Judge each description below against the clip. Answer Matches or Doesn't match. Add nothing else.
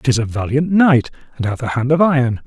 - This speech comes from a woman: Doesn't match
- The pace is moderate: Doesn't match